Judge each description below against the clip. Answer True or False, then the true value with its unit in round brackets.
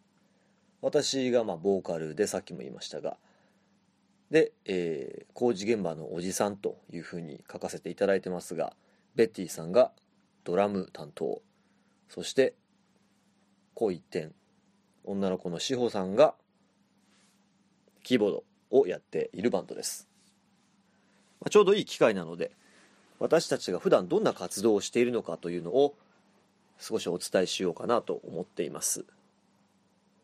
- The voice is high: False (120 Hz)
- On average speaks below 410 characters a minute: True (285 characters per minute)